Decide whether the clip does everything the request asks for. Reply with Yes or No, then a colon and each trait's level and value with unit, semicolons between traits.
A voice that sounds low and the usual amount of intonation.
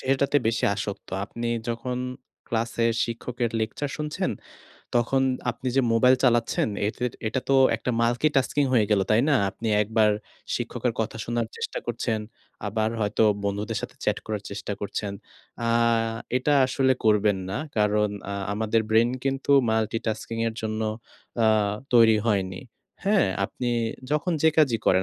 Yes: low, 115 Hz; average, 3.1 semitones